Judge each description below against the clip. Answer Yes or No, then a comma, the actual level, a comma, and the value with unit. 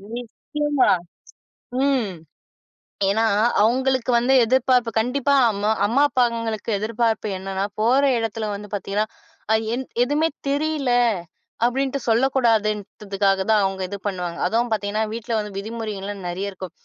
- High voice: Yes, high, 225 Hz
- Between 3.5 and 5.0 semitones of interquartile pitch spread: Yes, average, 3.9 semitones